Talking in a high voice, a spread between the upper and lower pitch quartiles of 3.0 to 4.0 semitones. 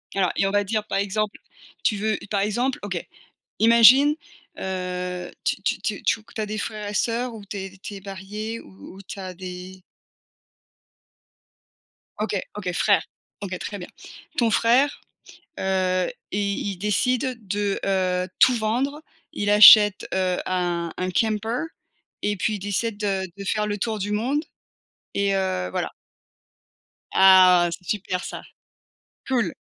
No: high, 205 Hz; narrow, 2.6 semitones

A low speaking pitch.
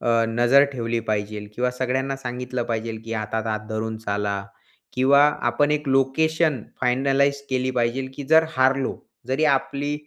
Yes: low, 125 Hz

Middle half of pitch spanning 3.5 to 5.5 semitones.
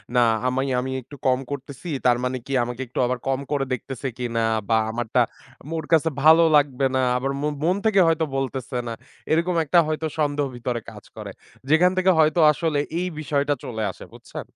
Yes: average, 3.8 semitones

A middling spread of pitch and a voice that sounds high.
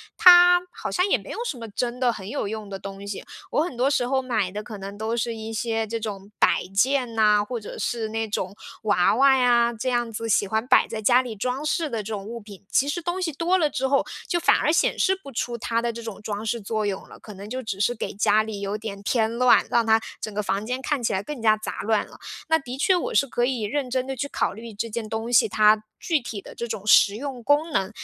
Yes: average, 3.6 semitones; high, 230 Hz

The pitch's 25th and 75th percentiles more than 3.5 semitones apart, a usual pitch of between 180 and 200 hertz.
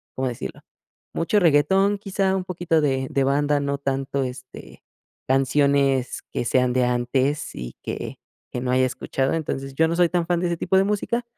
No: average, 4.7 semitones; medium, 140 Hz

